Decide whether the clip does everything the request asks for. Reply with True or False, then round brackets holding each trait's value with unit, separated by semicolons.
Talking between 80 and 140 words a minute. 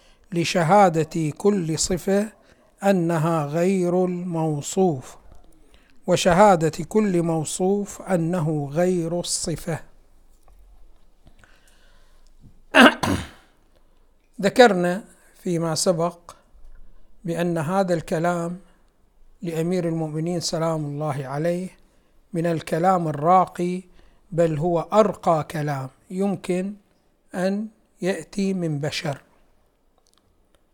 False (70 wpm)